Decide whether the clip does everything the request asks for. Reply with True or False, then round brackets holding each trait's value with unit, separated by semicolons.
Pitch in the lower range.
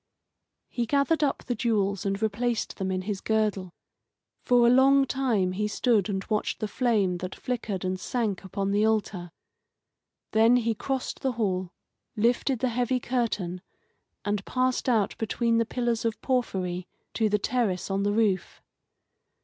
False (220 Hz)